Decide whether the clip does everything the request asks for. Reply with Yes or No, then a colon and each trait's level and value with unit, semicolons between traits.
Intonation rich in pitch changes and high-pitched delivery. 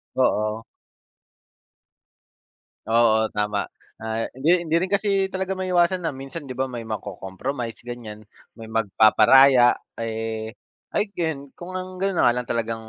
No: wide, 7.4 semitones; low, 120 Hz